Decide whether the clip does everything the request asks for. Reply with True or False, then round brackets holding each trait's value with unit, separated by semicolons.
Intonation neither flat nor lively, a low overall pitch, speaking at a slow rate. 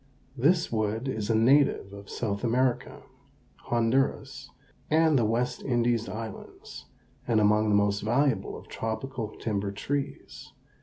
True (3.6 semitones; 115 Hz; 125 wpm)